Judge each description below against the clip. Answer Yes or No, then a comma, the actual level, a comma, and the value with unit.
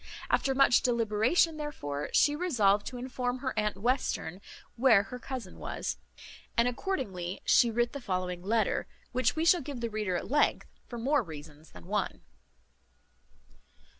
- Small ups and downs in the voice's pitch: No, average, 5.2 semitones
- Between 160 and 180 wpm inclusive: No, average, 150 wpm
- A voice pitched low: No, high, 235 Hz